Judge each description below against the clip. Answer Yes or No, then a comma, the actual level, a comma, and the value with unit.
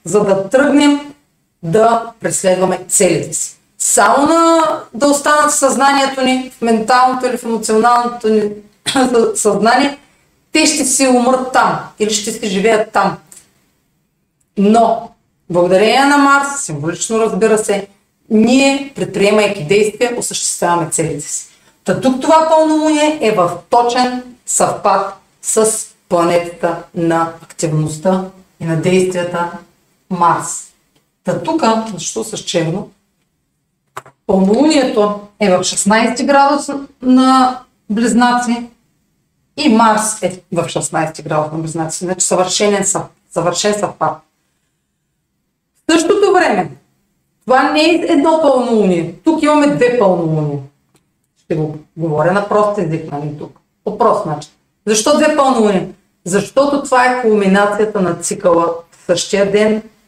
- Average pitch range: No, wide, 6.3 semitones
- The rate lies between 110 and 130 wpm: Yes, average, 120 wpm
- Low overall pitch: No, high, 210 Hz